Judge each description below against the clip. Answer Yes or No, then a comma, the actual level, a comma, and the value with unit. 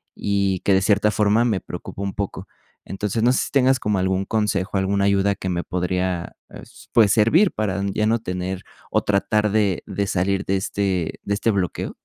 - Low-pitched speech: Yes, low, 100 Hz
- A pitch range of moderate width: No, narrow, 2.0 semitones